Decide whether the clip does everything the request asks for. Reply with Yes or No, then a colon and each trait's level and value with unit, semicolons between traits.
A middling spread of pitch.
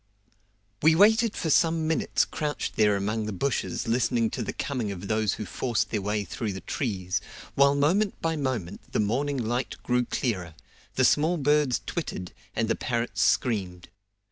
No: wide, 5.8 semitones